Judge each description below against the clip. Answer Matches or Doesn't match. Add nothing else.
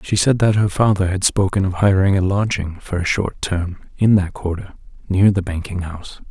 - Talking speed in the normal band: Doesn't match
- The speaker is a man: Matches